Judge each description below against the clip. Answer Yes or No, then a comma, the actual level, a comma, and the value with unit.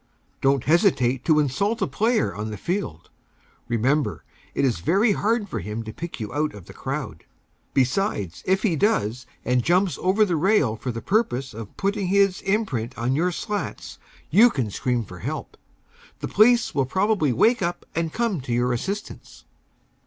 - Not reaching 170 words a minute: No, average, 175 wpm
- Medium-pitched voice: Yes, medium, 155 Hz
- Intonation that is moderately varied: No, wide, 8.8 semitones